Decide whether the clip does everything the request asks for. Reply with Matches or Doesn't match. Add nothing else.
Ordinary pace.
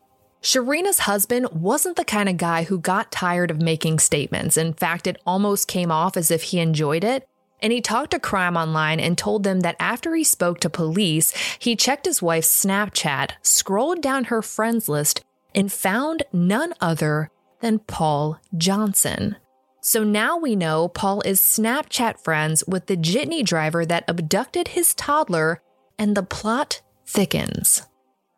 Matches